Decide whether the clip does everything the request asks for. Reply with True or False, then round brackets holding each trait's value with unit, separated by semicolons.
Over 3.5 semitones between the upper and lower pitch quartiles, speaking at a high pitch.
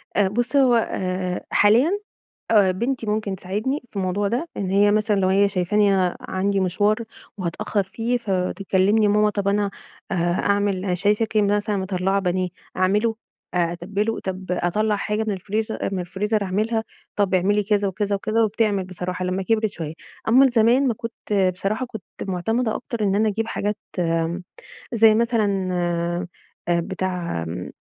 False (2.7 semitones; 200 Hz)